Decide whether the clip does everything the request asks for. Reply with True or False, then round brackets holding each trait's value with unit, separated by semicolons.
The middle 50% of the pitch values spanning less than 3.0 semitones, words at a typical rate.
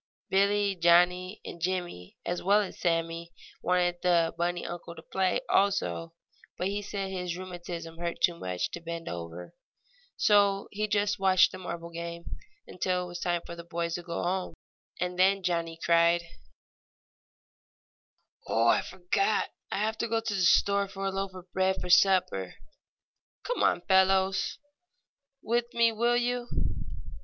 True (2.6 semitones; 155 wpm)